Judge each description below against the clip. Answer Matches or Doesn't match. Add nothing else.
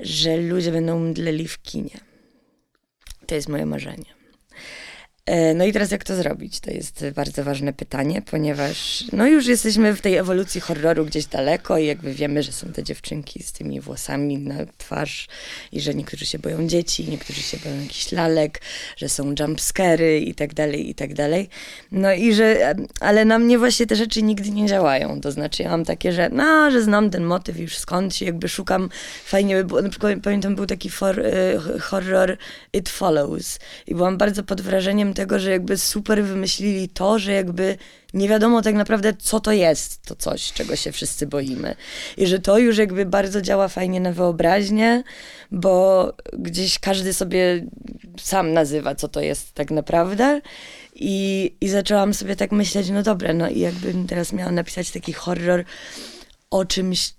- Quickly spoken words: Matches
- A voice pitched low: Doesn't match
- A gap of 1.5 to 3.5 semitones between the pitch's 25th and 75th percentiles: Doesn't match